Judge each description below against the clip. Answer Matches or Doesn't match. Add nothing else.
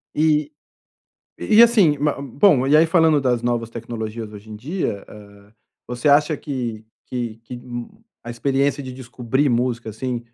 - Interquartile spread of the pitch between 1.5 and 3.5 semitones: Doesn't match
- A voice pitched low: Matches